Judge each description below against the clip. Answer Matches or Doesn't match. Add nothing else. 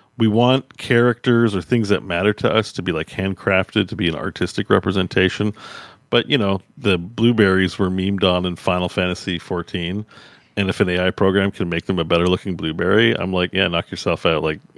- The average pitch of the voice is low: Matches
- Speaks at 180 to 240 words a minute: Matches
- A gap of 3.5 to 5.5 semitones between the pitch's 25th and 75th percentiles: Doesn't match